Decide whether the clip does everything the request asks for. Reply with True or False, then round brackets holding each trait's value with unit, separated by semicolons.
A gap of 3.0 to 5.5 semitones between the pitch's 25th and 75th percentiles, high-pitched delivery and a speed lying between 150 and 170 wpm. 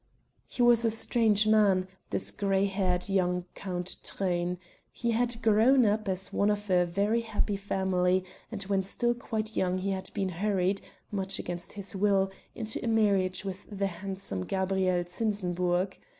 False (2.4 semitones; 195 Hz; 160 wpm)